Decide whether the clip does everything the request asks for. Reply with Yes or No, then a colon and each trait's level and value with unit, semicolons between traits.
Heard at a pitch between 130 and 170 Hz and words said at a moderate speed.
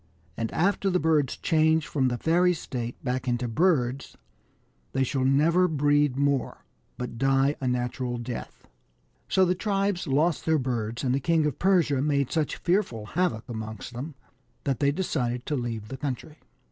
Yes: medium, 140 Hz; average, 165 wpm